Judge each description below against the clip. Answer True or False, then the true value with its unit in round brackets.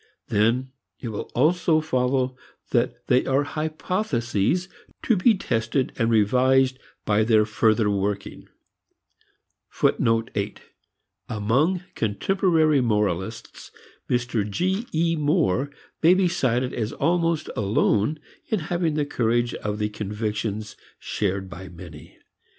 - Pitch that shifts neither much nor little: False (6.8 semitones)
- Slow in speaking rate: True (110 wpm)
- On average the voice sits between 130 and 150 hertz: False (120 Hz)